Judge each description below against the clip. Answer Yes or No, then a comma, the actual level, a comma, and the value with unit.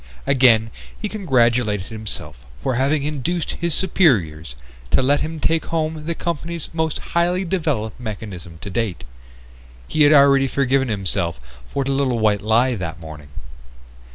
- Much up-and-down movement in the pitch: Yes, wide, 6.5 semitones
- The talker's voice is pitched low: Yes, low, 130 Hz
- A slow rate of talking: No, average, 145 wpm